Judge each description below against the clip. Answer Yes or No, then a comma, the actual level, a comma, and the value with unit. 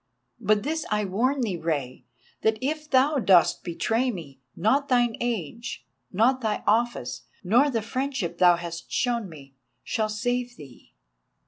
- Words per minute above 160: No, average, 145 wpm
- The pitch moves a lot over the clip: Yes, wide, 6.2 semitones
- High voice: Yes, high, 220 Hz